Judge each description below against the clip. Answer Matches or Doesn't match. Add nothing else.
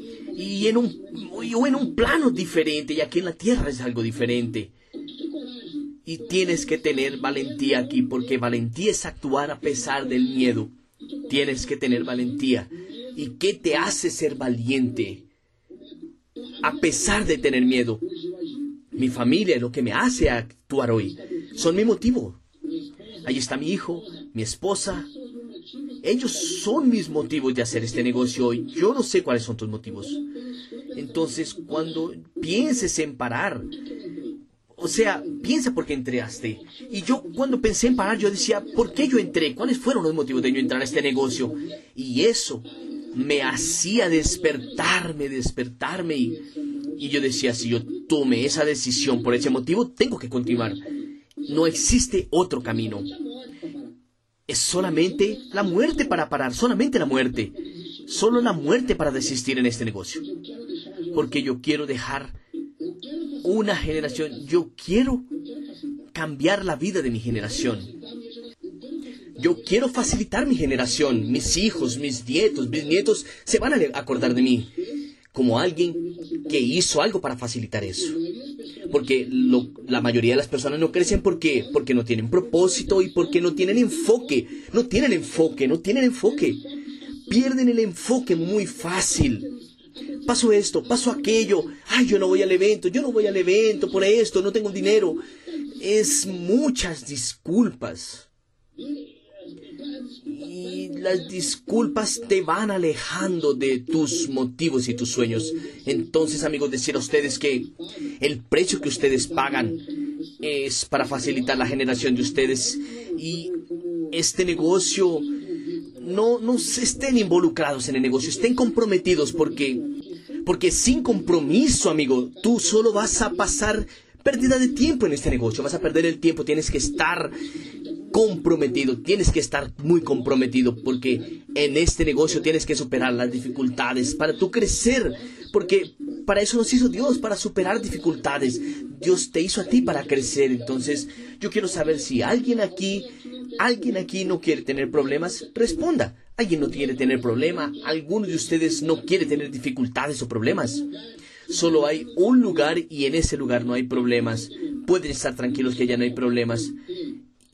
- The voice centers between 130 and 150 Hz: Doesn't match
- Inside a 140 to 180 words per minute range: Matches